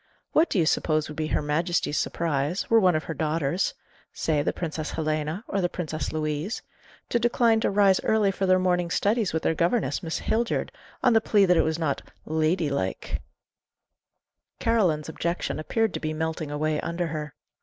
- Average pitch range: Yes, average, 4.0 semitones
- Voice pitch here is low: No, medium, 165 Hz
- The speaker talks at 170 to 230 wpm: Yes, average, 185 wpm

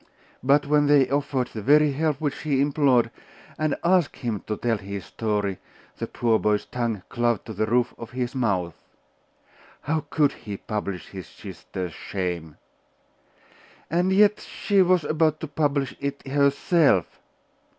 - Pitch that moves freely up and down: Yes, wide, 5.7 semitones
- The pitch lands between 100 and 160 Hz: Yes, low, 135 Hz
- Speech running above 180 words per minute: No, average, 150 wpm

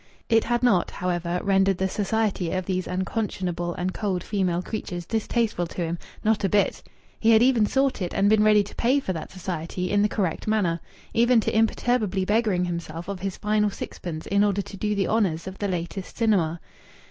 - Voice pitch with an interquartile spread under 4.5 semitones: Yes, average, 3.2 semitones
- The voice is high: Yes, high, 195 Hz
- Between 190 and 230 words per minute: Yes, average, 195 wpm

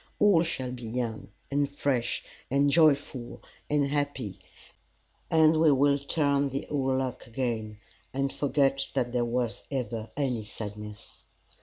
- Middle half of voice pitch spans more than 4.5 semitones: No, average, 3.1 semitones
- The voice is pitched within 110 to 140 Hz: Yes, low, 135 Hz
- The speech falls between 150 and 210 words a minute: No, slow, 135 wpm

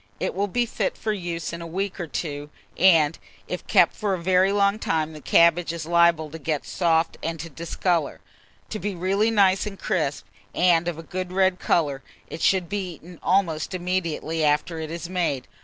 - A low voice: No, medium, 170 Hz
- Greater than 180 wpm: Yes, average, 190 wpm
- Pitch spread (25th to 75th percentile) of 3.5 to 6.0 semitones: No, average, 2.7 semitones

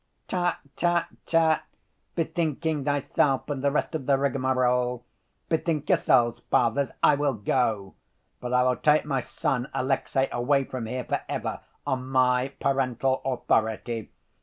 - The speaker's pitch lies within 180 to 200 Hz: No, low, 130 Hz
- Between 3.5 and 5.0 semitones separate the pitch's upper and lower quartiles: No, average, 2.7 semitones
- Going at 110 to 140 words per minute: Yes, slow, 135 wpm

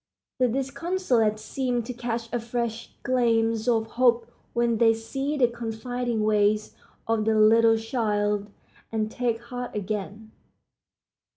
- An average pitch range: No, narrow, 1.9 semitones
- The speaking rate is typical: No, slow, 125 wpm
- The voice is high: Yes, high, 230 Hz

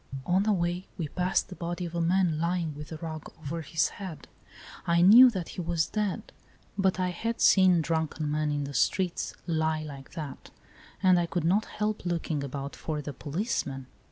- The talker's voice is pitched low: No, medium, 170 Hz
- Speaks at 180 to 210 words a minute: Yes, average, 190 wpm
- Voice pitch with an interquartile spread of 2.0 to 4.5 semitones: Yes, average, 3.0 semitones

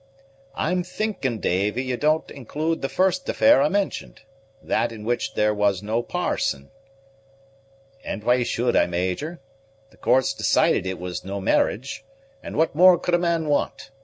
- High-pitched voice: No, low, 130 Hz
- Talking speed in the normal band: Yes, average, 160 wpm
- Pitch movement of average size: No, wide, 8.2 semitones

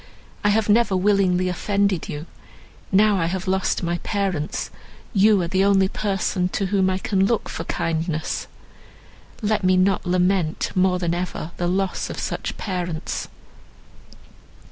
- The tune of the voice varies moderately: No, narrow, 2.0 semitones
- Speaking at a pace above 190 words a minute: No, average, 145 wpm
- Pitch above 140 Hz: Yes, high, 190 Hz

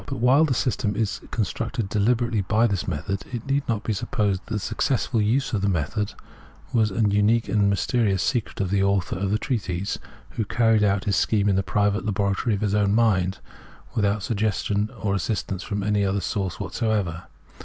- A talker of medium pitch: No, low, 105 Hz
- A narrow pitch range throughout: Yes, narrow, 2.3 semitones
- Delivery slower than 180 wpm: No, average, 195 wpm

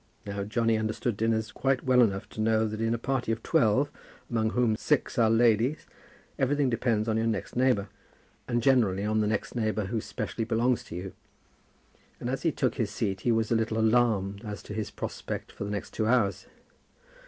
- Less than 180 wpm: No, average, 200 wpm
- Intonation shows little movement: Yes, narrow, 2.0 semitones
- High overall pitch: No, low, 110 Hz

